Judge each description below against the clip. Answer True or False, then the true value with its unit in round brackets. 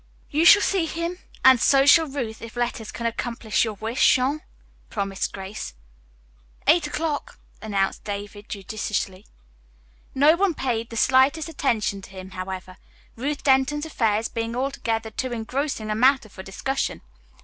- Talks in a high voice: True (235 Hz)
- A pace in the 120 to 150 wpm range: True (145 wpm)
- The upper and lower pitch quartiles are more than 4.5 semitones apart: True (5.1 semitones)